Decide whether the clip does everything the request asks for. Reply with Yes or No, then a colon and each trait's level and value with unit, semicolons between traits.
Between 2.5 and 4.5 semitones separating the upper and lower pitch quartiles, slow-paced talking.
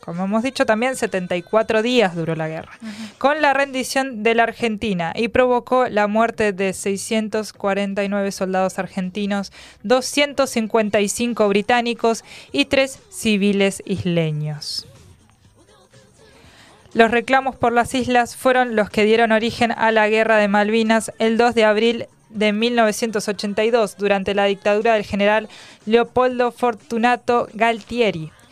Yes: average, 2.9 semitones; slow, 120 wpm